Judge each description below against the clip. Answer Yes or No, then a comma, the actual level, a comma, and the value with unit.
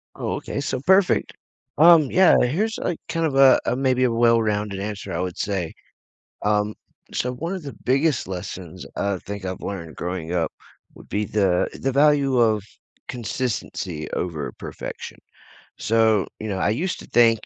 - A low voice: Yes, low, 110 Hz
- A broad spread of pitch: Yes, wide, 5.9 semitones